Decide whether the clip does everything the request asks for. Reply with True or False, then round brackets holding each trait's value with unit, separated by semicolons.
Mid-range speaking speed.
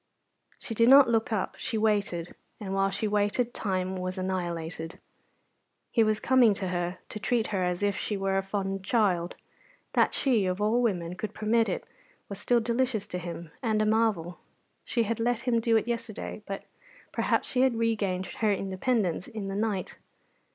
True (180 wpm)